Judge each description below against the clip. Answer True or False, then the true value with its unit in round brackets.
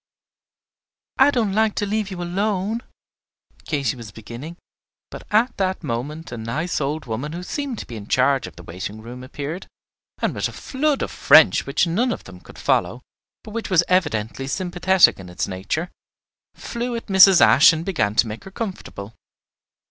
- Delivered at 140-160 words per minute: False (180 wpm)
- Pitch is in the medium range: True (165 Hz)